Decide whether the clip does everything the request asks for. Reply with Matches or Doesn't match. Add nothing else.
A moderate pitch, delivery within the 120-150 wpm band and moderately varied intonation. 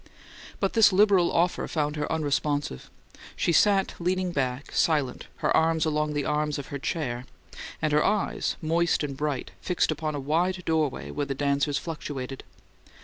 Doesn't match